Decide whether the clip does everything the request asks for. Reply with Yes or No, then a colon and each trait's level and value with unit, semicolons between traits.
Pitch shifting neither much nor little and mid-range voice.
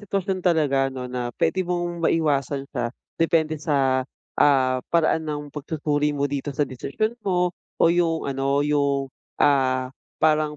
Yes: average, 3.2 semitones; medium, 145 Hz